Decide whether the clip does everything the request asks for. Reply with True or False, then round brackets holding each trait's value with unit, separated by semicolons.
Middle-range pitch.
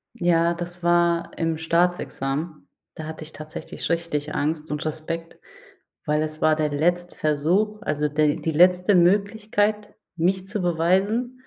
True (170 Hz)